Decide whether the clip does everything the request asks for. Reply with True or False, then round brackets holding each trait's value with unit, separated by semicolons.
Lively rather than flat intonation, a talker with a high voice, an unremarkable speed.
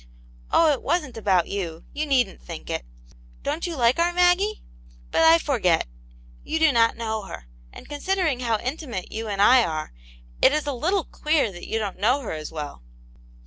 True (7.7 semitones; 250 Hz; 185 wpm)